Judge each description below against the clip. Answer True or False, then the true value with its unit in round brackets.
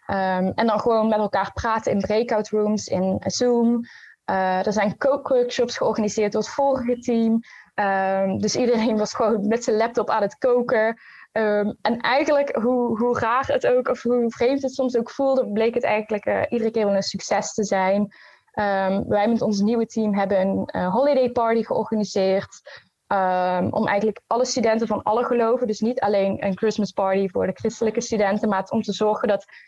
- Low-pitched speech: False (220 Hz)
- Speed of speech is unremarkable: True (190 wpm)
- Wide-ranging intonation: False (3.0 semitones)